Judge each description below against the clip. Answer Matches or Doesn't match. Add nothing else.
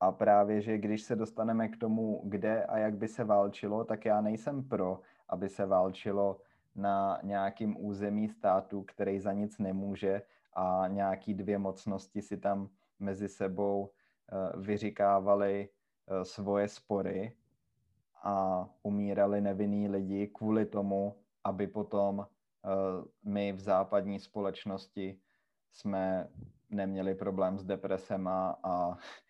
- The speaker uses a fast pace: Doesn't match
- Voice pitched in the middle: Doesn't match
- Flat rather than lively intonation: Matches